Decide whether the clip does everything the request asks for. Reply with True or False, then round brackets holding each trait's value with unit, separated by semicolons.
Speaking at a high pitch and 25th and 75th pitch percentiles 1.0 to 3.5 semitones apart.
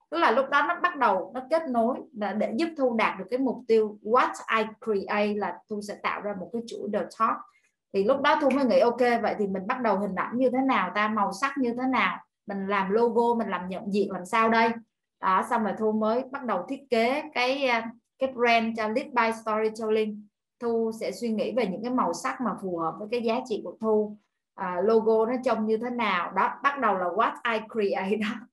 True (225 Hz; 3.0 semitones)